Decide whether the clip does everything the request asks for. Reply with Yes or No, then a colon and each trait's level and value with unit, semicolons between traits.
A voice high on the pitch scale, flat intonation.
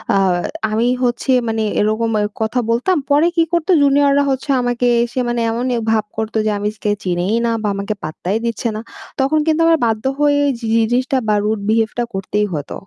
No: high, 230 Hz; average, 4.1 semitones